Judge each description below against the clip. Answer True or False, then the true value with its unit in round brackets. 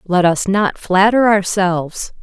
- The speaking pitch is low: False (190 Hz)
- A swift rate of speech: False (135 wpm)